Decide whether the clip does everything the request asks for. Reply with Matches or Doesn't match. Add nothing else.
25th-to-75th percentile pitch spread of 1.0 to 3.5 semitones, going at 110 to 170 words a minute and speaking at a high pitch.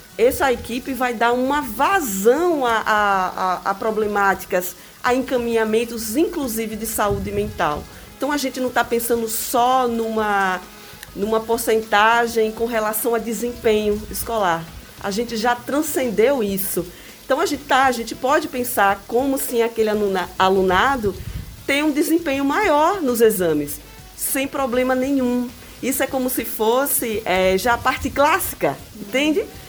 Doesn't match